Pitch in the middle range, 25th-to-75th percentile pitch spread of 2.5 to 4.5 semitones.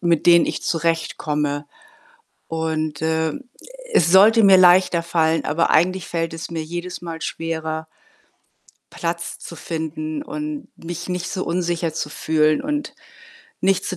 No: medium, 165 Hz; narrow, 1.7 semitones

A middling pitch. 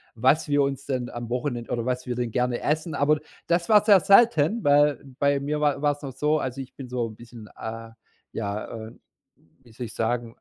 No: low, 130 Hz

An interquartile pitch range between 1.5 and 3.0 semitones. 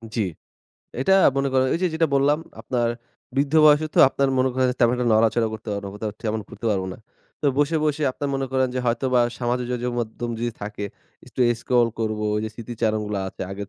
No: average, 3.7 semitones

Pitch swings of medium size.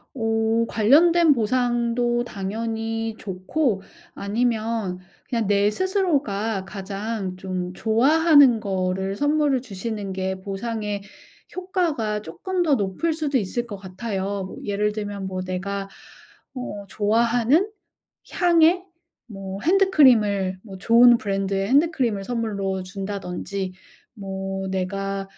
Yes: average, 4.0 semitones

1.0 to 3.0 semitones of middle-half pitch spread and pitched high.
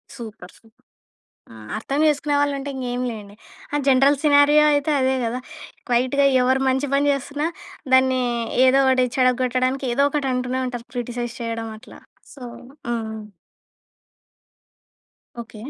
Yes: narrow, 2.6 semitones; very high, 260 Hz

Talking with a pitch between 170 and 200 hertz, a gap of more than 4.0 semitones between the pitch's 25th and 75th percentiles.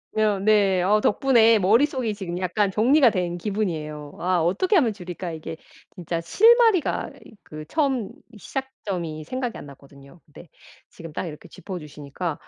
Yes: high, 190 Hz; wide, 5.5 semitones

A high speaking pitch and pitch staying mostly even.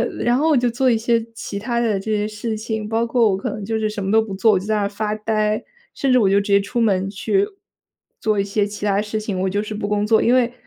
Yes: high, 215 Hz; narrow, 2.1 semitones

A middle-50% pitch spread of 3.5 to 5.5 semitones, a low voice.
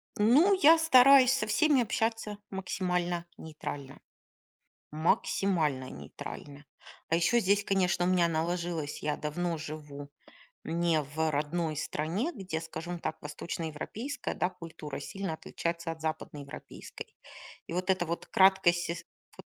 No: average, 3.8 semitones; medium, 170 Hz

